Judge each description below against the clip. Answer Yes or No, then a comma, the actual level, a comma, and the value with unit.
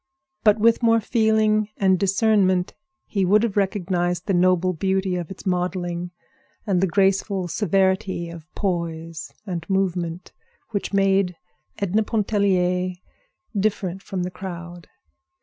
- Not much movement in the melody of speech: Yes, narrow, 2.1 semitones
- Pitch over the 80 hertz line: Yes, high, 190 Hz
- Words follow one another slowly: Yes, slow, 125 wpm